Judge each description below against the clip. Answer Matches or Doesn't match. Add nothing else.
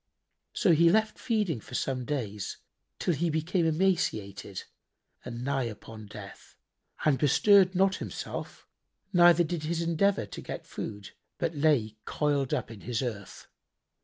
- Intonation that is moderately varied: Doesn't match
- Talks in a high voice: Doesn't match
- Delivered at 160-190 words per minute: Doesn't match